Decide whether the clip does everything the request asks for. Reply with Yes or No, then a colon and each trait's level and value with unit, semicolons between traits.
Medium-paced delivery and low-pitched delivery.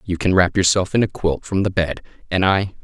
No: fast, 255 wpm; very low, 90 Hz